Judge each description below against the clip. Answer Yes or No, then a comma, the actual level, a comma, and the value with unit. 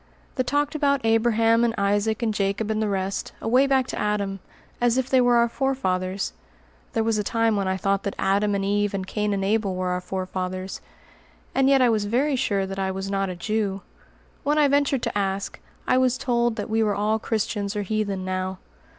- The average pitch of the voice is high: Yes, high, 210 Hz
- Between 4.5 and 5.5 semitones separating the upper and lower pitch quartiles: No, average, 3.4 semitones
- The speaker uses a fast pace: Yes, fast, 215 wpm